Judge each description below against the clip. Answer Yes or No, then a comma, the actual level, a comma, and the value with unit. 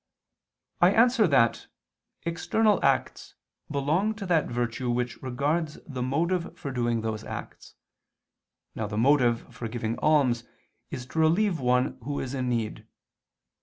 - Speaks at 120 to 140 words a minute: Yes, slow, 135 wpm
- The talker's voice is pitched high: No, low, 135 Hz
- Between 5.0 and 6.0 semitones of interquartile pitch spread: Yes, wide, 5.6 semitones